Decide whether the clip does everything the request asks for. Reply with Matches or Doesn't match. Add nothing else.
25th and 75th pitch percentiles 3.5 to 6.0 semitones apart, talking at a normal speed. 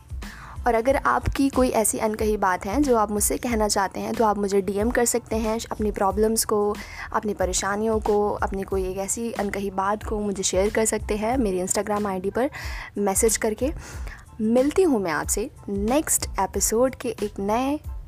Doesn't match